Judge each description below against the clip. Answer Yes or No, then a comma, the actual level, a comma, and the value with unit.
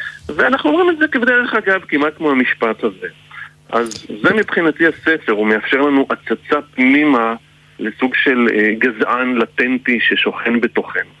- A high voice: No, medium, 140 Hz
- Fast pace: No, average, 135 wpm